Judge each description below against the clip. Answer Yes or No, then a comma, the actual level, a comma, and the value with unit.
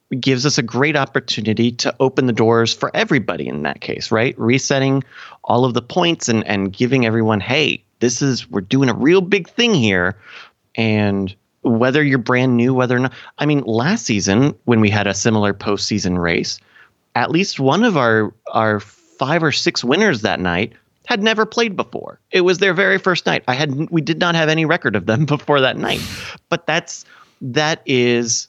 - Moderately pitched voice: No, low, 125 Hz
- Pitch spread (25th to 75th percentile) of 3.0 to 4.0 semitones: No, average, 5.0 semitones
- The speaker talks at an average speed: Yes, average, 195 wpm